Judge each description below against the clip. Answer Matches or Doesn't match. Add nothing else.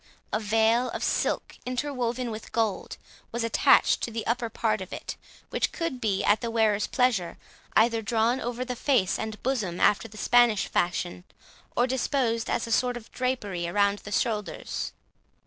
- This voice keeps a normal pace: Matches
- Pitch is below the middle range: Doesn't match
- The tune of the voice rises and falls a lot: Doesn't match